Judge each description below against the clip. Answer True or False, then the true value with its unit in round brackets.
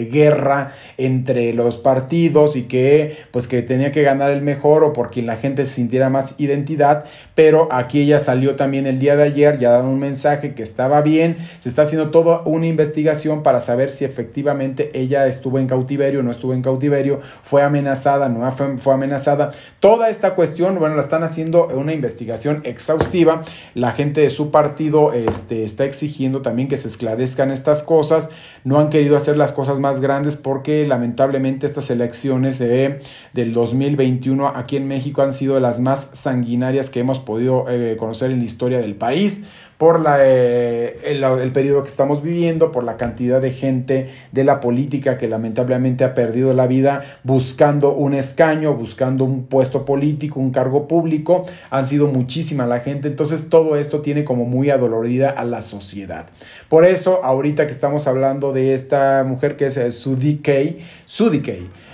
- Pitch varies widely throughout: False (2.5 semitones)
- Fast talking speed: False (175 wpm)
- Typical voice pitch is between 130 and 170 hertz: True (140 Hz)